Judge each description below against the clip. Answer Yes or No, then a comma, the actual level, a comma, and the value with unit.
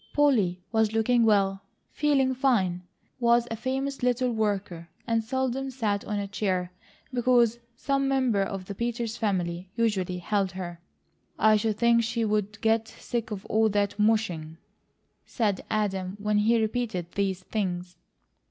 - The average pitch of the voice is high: Yes, high, 215 Hz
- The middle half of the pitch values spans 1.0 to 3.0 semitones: No, average, 3.6 semitones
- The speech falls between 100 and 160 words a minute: Yes, average, 145 wpm